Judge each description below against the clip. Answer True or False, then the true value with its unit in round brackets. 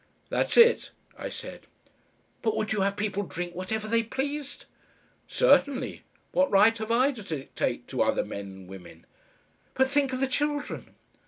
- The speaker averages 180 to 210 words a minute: False (160 wpm)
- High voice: True (225 Hz)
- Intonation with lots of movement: True (5.9 semitones)